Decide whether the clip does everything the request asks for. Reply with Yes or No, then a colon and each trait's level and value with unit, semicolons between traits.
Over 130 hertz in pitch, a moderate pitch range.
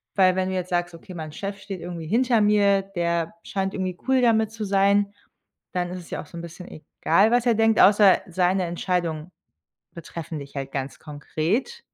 Yes: medium, 185 Hz; average, 3.2 semitones